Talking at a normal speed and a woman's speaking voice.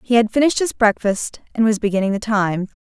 No: fast, 210 wpm; female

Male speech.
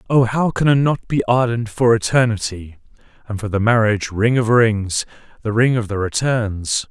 Yes: male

